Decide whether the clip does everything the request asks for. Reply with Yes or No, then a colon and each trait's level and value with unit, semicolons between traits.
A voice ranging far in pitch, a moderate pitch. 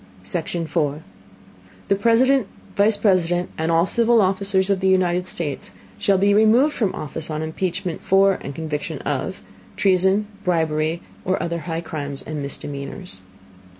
No: average, 3.8 semitones; medium, 180 Hz